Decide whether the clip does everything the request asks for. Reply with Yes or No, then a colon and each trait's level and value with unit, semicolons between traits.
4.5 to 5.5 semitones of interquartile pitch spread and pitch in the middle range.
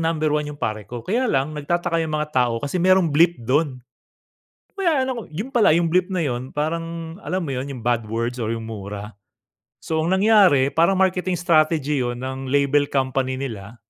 Yes: average, 5.0 semitones; medium, 150 Hz